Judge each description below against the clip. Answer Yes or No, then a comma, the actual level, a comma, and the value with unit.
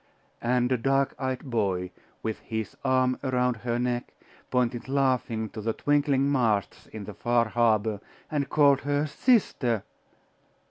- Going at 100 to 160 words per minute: Yes, average, 140 wpm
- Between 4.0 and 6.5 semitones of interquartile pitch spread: No, average, 3.4 semitones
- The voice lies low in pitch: Yes, low, 125 Hz